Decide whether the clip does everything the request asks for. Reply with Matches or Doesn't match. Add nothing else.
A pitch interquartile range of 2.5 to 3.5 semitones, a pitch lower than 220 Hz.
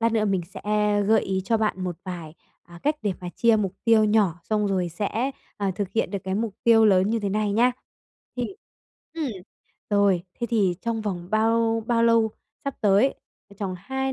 Matches